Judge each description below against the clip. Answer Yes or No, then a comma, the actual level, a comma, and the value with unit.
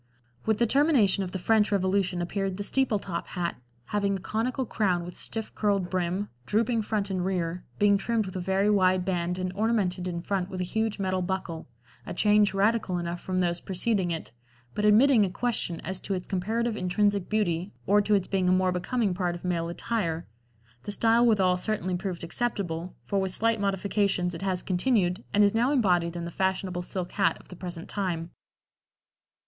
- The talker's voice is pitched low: No, high, 190 Hz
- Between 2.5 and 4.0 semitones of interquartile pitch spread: Yes, average, 2.8 semitones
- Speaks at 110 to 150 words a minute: No, average, 195 wpm